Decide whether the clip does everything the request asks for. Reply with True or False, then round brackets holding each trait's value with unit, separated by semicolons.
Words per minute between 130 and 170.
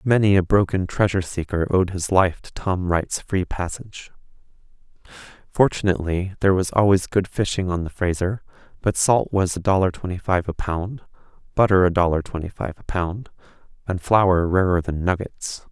True (165 wpm)